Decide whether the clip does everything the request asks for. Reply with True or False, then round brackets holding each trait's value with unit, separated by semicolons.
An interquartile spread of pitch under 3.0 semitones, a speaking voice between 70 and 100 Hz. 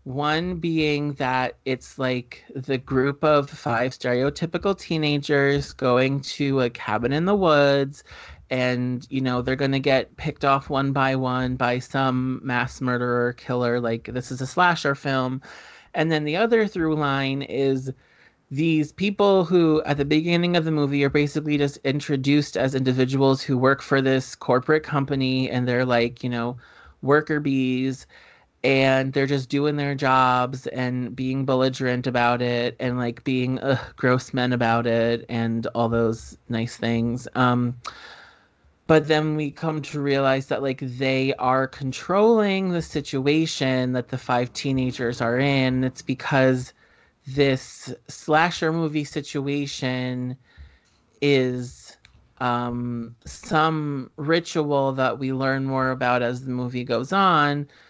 False (2.6 semitones; 135 Hz)